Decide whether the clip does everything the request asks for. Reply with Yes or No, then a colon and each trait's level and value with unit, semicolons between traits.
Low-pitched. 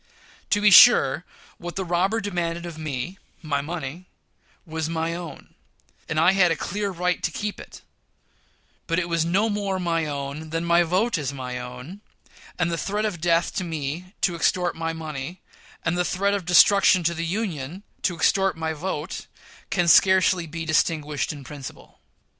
No: medium, 170 Hz